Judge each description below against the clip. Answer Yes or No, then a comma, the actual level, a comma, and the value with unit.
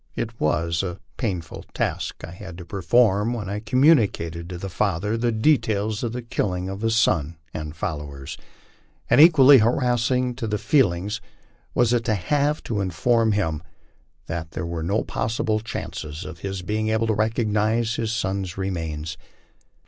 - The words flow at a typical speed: Yes, average, 160 wpm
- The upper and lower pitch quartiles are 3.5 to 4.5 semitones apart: No, average, 5.1 semitones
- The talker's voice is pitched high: No, low, 105 Hz